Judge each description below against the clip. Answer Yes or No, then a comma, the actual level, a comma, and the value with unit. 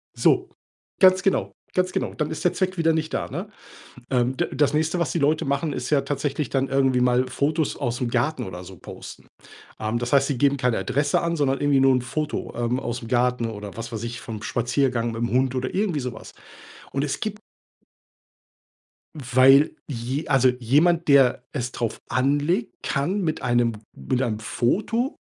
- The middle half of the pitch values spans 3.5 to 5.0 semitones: Yes, average, 3.9 semitones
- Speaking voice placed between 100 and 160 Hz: Yes, low, 135 Hz